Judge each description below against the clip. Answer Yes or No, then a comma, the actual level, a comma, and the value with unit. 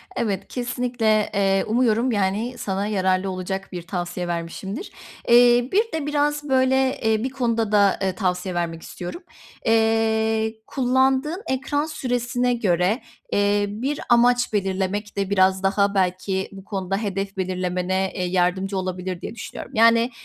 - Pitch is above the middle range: Yes, high, 210 Hz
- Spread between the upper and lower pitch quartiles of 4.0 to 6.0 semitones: Yes, average, 4.4 semitones